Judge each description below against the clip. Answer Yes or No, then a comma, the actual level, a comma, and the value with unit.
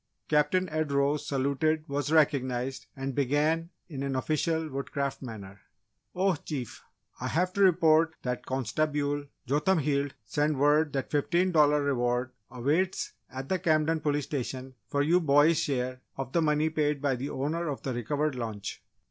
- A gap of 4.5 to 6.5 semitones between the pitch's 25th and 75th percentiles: No, average, 2.8 semitones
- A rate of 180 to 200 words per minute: No, average, 155 wpm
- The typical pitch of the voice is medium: Yes, medium, 145 Hz